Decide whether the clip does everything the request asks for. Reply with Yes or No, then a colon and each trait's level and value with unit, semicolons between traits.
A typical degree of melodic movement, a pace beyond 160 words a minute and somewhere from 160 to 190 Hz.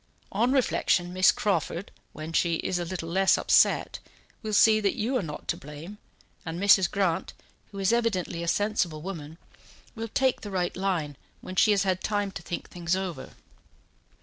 Yes: average, 3.4 semitones; average, 175 wpm; medium, 185 Hz